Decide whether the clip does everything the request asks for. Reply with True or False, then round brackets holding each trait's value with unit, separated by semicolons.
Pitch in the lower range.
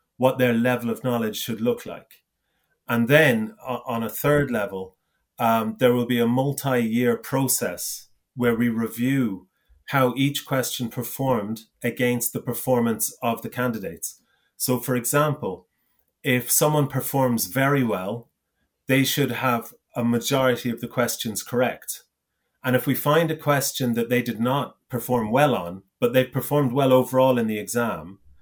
True (125 Hz)